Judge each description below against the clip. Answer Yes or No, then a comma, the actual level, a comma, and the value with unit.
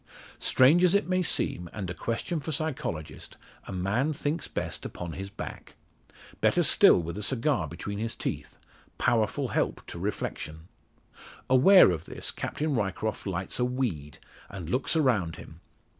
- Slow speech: No, average, 155 wpm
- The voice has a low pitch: Yes, low, 110 Hz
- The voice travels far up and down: Yes, wide, 8.2 semitones